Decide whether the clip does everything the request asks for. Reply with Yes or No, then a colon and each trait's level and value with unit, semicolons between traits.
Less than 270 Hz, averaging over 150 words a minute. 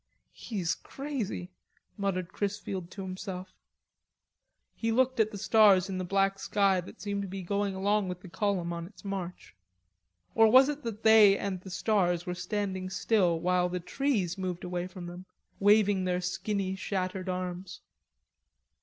Yes: high, 190 Hz; average, 160 wpm